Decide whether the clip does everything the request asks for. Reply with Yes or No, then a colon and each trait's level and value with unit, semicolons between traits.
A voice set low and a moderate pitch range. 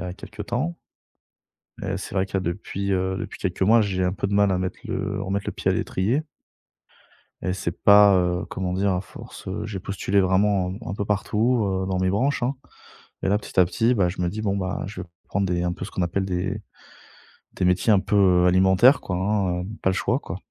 No: very low, 95 Hz; narrow, 1.8 semitones